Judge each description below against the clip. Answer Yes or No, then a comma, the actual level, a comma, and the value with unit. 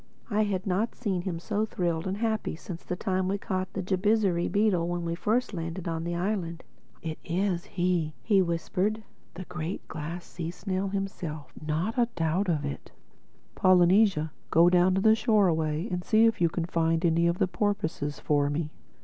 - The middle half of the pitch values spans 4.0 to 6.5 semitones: No, average, 3.2 semitones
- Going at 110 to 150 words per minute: No, average, 175 wpm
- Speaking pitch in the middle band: Yes, medium, 180 Hz